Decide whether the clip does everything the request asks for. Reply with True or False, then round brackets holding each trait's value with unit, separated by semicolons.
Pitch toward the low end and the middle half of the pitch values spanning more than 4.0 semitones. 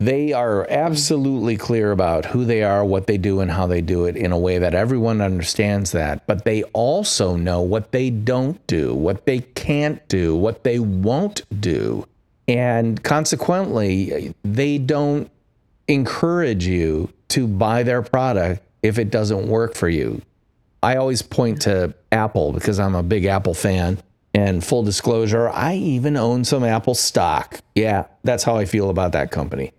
True (110 Hz; 4.9 semitones)